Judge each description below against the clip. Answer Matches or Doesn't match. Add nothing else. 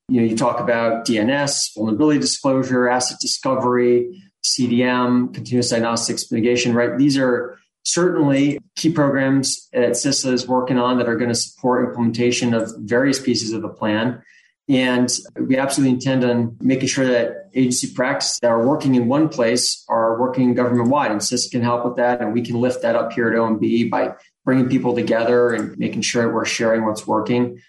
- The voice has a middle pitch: Doesn't match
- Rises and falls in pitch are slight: Matches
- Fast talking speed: Doesn't match